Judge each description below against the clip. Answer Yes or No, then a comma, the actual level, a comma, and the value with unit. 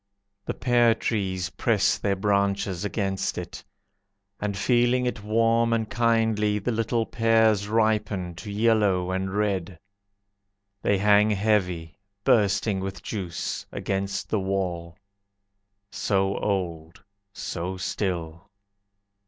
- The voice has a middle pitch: No, low, 100 Hz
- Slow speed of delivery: Yes, slow, 110 wpm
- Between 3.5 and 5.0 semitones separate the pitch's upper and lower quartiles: No, average, 2.9 semitones